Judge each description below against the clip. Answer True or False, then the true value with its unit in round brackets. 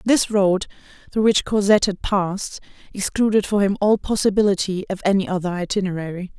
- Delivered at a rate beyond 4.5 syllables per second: True (5.8 syllables/s)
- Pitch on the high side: True (195 Hz)